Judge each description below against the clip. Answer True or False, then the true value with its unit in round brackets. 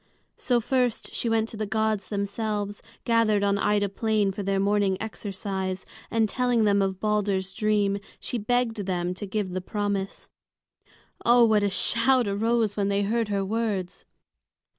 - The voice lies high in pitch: True (205 Hz)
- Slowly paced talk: False (160 wpm)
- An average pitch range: False (2.1 semitones)